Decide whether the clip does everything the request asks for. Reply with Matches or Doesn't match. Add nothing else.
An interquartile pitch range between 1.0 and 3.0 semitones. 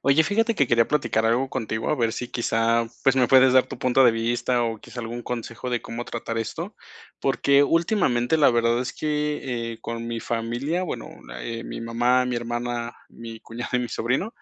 Matches